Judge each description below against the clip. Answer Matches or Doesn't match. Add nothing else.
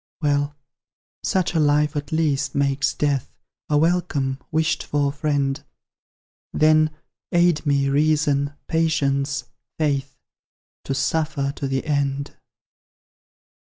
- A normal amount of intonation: Doesn't match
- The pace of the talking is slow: Matches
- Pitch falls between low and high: Matches